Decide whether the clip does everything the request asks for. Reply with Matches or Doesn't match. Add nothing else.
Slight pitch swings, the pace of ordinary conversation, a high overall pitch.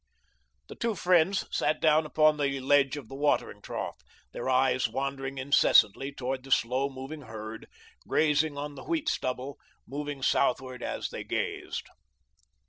Doesn't match